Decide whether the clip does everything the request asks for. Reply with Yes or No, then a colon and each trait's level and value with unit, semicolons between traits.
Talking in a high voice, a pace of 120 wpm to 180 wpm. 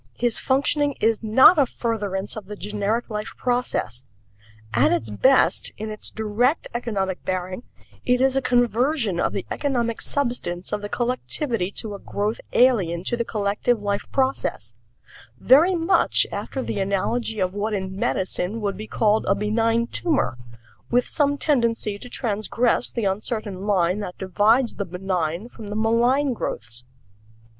Yes: high, 220 Hz; average, 150 wpm